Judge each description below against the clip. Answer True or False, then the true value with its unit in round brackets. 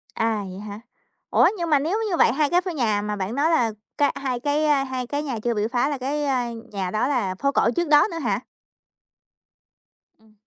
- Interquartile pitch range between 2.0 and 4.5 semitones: False (5.0 semitones)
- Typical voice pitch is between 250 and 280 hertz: True (265 Hz)